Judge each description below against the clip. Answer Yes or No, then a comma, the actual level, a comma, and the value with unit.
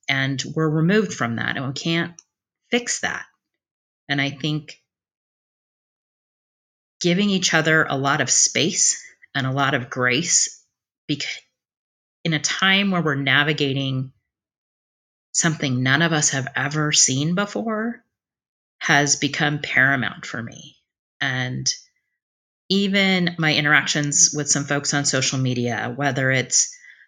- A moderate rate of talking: No, slow, 125 wpm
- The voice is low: No, medium, 145 Hz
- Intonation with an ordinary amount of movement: Yes, average, 3.8 semitones